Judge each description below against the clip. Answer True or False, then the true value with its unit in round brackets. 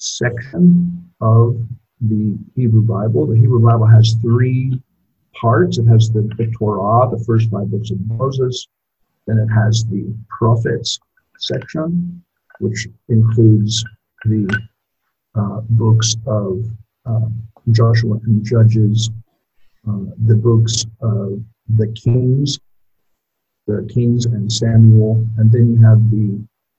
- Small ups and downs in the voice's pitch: True (1.4 semitones)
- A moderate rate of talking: False (115 wpm)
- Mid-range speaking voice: False (115 Hz)